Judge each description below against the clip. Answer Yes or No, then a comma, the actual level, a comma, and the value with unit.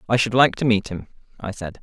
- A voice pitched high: No, low, 110 Hz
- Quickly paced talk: Yes, fast, 265 wpm